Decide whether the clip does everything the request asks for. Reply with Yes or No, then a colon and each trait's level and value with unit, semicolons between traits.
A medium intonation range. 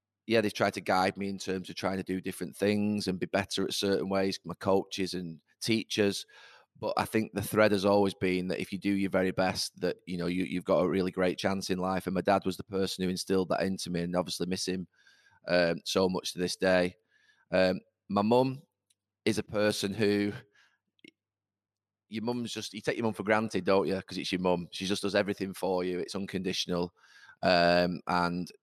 No: narrow, 1.7 semitones